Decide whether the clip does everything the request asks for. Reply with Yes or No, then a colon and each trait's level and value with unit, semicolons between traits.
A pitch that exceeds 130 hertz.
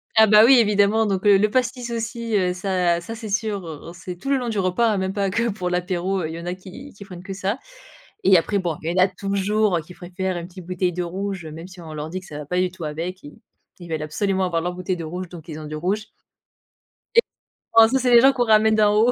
Yes: high, 190 Hz